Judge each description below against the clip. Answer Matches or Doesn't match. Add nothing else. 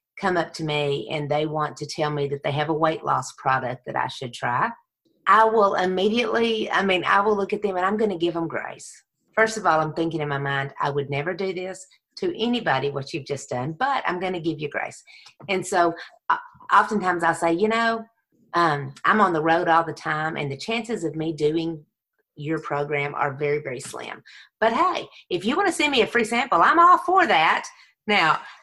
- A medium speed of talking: Doesn't match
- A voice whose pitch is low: Doesn't match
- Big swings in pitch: Matches